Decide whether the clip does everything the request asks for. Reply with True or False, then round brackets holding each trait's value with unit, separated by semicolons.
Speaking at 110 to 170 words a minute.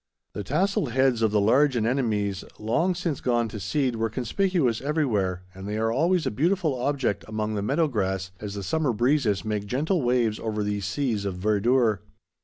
False (185 wpm)